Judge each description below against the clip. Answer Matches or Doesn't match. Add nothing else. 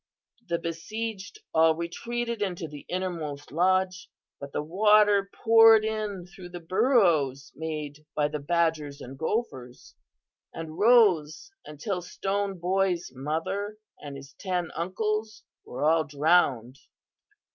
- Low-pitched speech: Doesn't match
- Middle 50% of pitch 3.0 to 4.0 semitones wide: Doesn't match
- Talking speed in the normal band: Doesn't match